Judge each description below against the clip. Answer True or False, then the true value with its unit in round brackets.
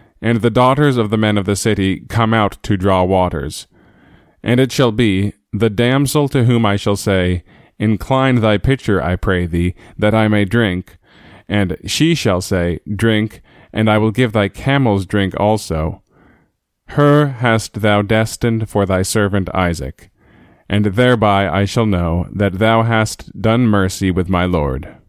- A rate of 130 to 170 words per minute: True (165 wpm)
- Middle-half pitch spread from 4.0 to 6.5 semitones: False (3.5 semitones)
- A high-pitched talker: False (105 Hz)